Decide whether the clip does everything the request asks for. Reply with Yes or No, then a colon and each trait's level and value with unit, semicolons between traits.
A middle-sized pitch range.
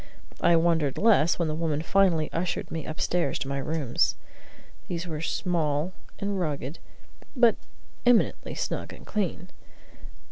Yes: average, 3.0 semitones